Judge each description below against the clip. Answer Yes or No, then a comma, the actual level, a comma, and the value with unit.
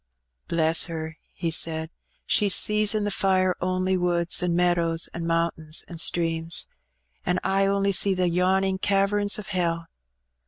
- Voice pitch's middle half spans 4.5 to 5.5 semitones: No, narrow, 2.6 semitones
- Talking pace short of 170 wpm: Yes, average, 150 wpm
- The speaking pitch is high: No, medium, 180 Hz